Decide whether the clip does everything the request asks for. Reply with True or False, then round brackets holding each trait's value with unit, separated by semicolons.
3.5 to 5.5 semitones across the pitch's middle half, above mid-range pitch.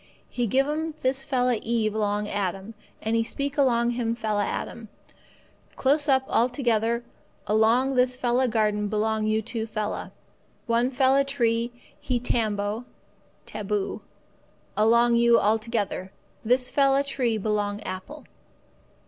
False (3.0 semitones; 235 Hz)